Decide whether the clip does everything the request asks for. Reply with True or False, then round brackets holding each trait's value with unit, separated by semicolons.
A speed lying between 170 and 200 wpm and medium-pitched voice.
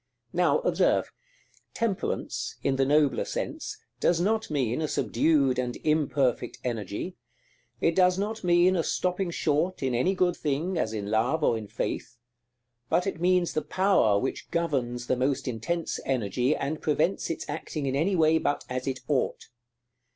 False (160 wpm; 150 Hz)